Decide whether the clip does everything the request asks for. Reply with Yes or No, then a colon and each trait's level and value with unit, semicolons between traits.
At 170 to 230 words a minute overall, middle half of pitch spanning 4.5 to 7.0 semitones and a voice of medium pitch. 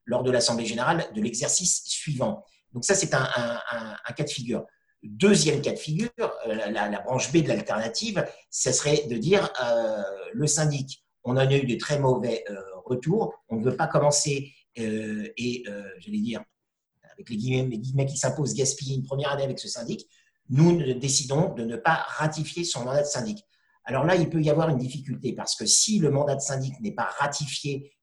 Yes: average, 205 wpm; average, 5.2 semitones; medium, 145 Hz